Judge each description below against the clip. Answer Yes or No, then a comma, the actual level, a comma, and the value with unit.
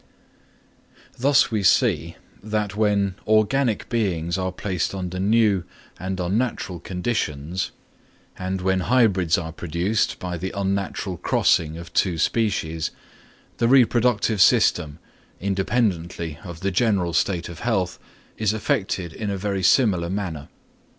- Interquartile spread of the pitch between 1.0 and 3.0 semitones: No, average, 3.6 semitones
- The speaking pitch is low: Yes, very low, 95 Hz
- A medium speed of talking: No, slow, 125 wpm